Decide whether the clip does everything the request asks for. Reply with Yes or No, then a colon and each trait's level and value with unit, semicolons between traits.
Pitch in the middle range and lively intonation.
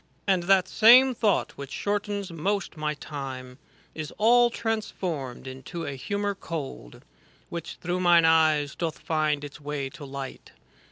Yes: medium, 165 Hz; wide, 5.8 semitones